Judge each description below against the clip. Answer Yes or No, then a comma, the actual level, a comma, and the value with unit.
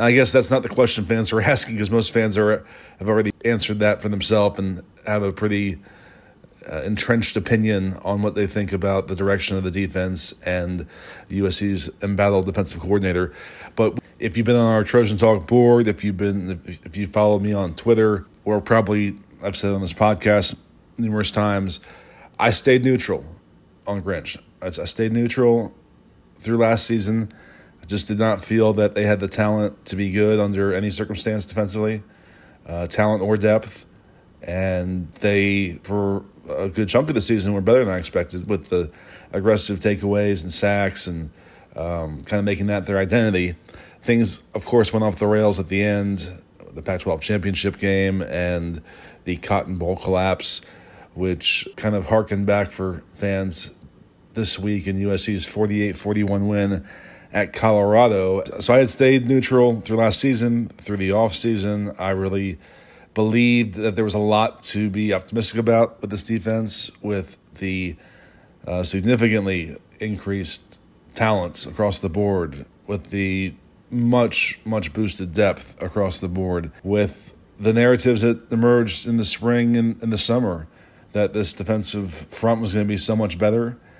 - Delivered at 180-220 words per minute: No, average, 165 wpm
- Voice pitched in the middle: No, low, 105 Hz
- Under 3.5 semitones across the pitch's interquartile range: Yes, narrow, 2.5 semitones